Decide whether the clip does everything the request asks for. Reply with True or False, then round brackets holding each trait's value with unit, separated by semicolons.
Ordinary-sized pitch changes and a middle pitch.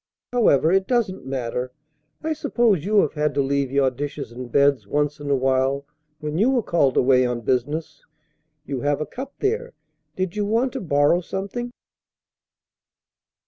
False (7.1 semitones; 145 Hz)